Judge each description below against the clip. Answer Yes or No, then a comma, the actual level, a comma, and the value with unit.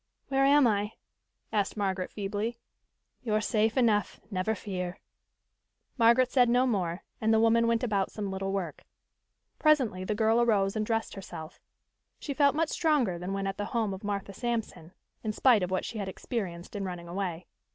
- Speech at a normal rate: Yes, average, 175 wpm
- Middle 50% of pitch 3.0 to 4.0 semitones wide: Yes, average, 3.4 semitones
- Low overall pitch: No, high, 210 Hz